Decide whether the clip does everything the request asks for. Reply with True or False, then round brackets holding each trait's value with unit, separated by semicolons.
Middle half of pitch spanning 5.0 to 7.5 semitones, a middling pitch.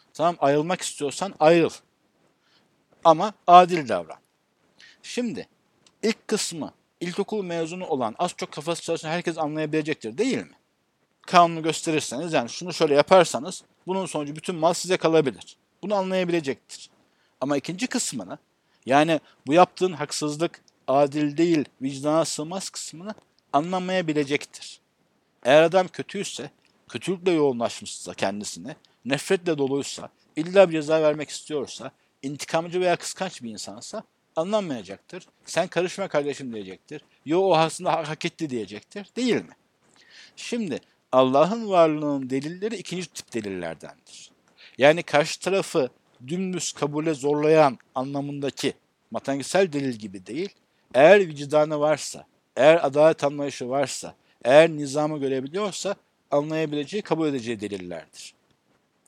False (4.3 semitones; 160 Hz)